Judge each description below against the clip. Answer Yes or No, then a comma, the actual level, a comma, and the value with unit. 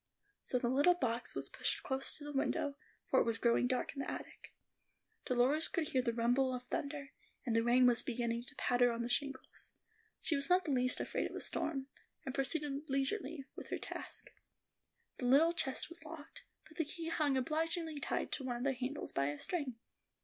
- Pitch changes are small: No, average, 3.5 semitones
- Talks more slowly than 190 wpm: No, fast, 205 wpm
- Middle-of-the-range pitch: No, very high, 270 Hz